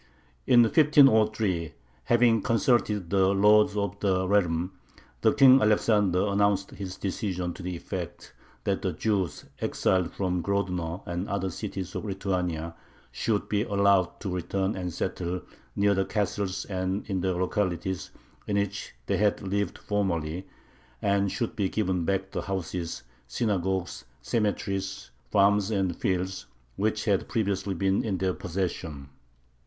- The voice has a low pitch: Yes, very low, 95 Hz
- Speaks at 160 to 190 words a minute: No, slow, 135 wpm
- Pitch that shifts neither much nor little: No, narrow, 2.1 semitones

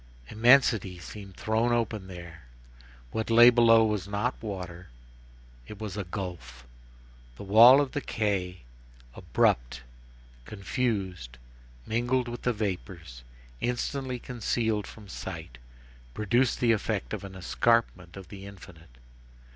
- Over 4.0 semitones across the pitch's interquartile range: Yes, average, 4.6 semitones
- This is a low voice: Yes, low, 105 Hz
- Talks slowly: Yes, slow, 120 wpm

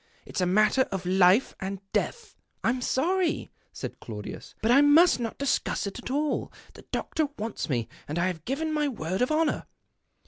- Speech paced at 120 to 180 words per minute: No, average, 195 wpm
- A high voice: Yes, high, 245 Hz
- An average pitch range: No, wide, 8.2 semitones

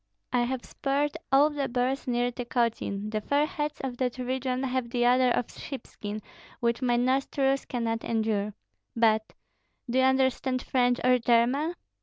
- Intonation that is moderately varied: No, narrow, 2.1 semitones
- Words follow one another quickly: No, average, 155 wpm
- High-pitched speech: Yes, very high, 250 Hz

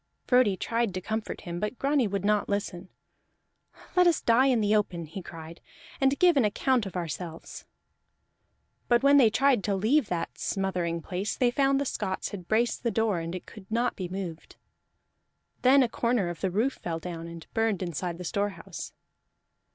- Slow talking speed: No, average, 180 wpm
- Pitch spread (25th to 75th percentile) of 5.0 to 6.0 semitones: Yes, average, 5.3 semitones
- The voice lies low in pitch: No, high, 205 Hz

